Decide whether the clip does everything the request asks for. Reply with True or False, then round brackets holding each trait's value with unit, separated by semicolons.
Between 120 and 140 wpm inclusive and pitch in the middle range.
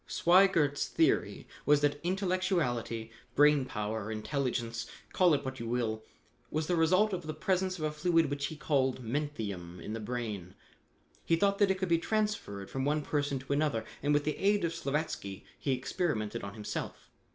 False (175 wpm; 145 Hz)